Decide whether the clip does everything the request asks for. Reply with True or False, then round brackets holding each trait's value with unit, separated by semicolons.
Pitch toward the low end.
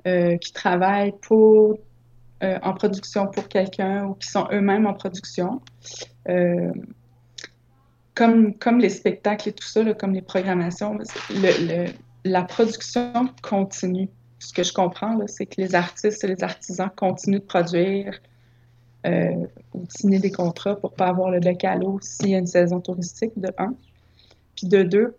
False (190 Hz)